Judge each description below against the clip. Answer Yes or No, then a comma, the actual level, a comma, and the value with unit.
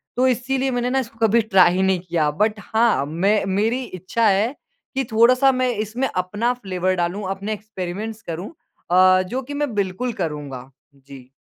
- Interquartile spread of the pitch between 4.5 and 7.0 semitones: Yes, average, 4.8 semitones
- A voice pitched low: No, high, 210 Hz